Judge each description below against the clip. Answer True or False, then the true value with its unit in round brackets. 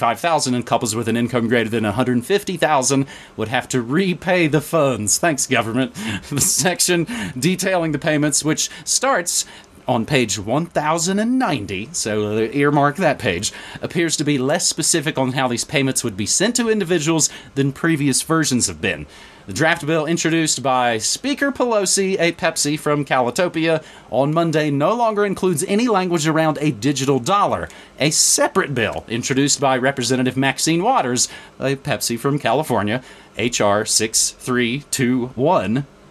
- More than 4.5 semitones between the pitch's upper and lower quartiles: True (5.2 semitones)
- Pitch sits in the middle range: True (145 Hz)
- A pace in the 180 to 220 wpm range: False (140 wpm)